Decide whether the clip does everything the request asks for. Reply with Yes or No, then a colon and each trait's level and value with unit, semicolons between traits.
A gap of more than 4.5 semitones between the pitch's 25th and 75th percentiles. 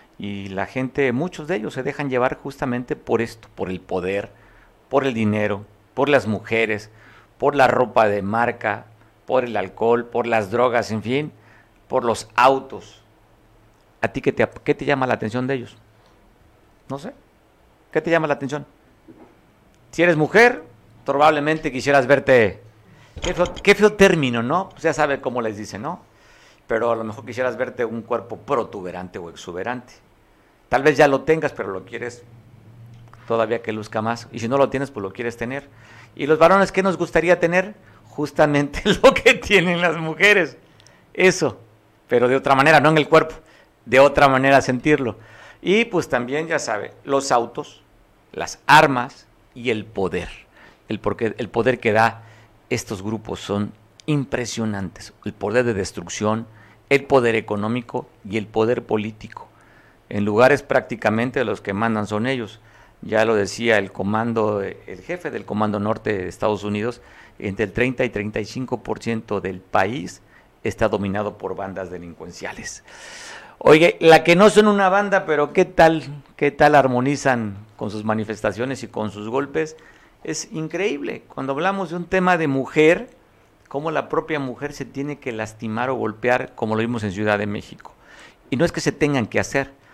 Yes: average, 4.9 semitones